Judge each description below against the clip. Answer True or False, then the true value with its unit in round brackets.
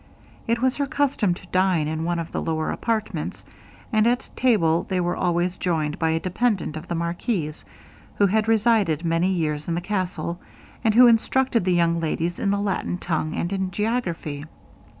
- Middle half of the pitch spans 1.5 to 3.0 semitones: False (4.6 semitones)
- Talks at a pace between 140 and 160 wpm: False (185 wpm)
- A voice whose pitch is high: False (180 Hz)